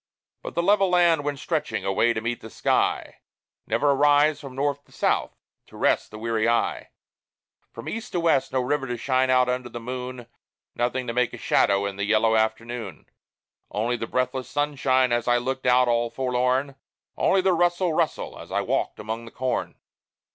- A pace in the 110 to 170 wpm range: No, average, 190 wpm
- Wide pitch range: No, average, 3.6 semitones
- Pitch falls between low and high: No, low, 125 Hz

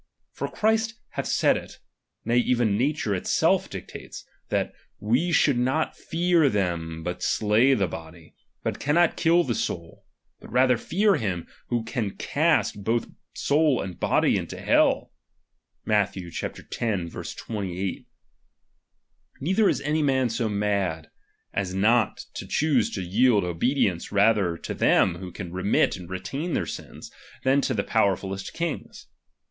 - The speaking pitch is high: No, low, 110 Hz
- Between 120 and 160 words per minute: Yes, average, 140 wpm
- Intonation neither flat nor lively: No, wide, 6.6 semitones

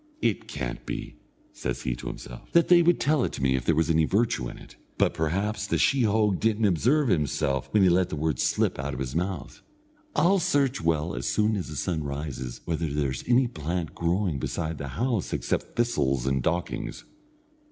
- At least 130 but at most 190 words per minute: No, average, 200 wpm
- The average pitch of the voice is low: Yes, very low, 85 Hz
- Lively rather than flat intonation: Yes, wide, 7.6 semitones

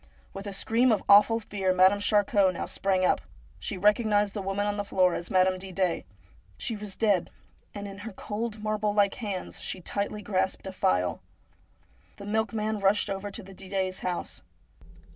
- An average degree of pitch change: No, narrow, 1.8 semitones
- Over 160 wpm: Yes, average, 175 wpm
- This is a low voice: No, high, 200 Hz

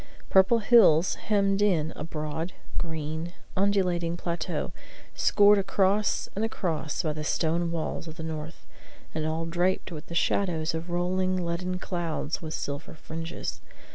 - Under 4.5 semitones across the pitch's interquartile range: Yes, average, 2.8 semitones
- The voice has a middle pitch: Yes, medium, 170 Hz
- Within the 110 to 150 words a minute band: Yes, average, 140 wpm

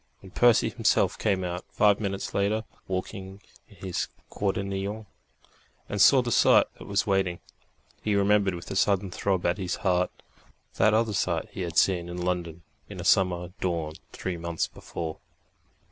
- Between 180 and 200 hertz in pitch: No, very low, 95 Hz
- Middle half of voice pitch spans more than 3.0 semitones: No, narrow, 2.5 semitones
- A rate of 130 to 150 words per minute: No, average, 160 wpm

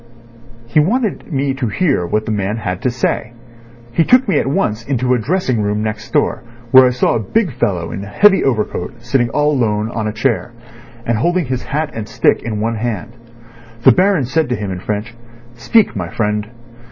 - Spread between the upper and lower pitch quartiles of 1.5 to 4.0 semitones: No, average, 4.6 semitones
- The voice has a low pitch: Yes, low, 120 Hz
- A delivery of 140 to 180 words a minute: No, average, 200 wpm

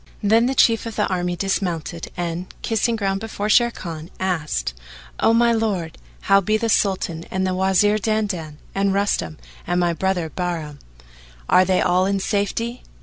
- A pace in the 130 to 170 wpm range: Yes, average, 160 wpm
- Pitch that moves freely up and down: No, average, 3.5 semitones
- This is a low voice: No, high, 190 Hz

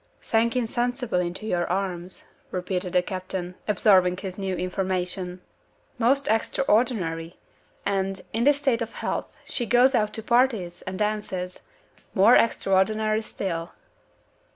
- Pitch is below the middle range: No, high, 195 Hz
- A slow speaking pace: Yes, slow, 125 wpm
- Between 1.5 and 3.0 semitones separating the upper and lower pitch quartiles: No, average, 4.0 semitones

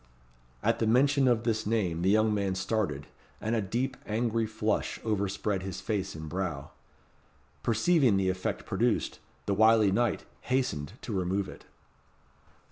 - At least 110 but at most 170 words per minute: Yes, average, 145 wpm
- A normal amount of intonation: Yes, average, 3.3 semitones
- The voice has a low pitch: Yes, low, 105 Hz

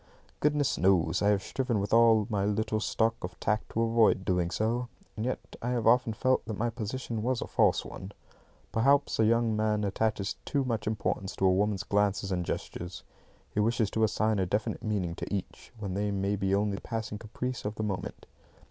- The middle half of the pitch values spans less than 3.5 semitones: Yes, narrow, 2.5 semitones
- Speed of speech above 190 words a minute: Yes, average, 200 wpm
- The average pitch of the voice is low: Yes, low, 110 Hz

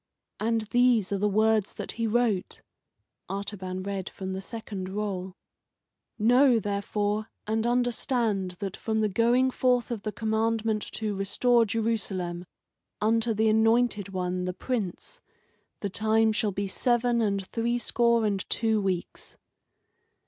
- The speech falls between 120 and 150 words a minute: Yes, slow, 135 wpm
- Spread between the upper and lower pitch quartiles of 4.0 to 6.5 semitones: No, average, 2.7 semitones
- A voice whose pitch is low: No, high, 215 Hz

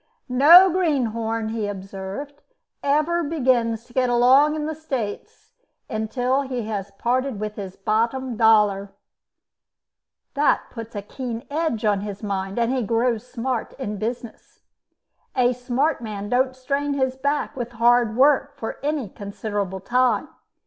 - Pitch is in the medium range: No, high, 240 Hz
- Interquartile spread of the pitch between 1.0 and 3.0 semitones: No, average, 3.9 semitones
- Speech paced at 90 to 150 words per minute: Yes, average, 140 wpm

